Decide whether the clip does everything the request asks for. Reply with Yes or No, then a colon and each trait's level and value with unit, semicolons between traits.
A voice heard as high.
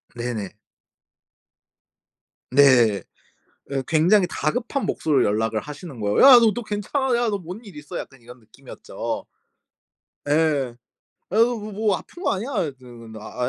No: medium, 150 Hz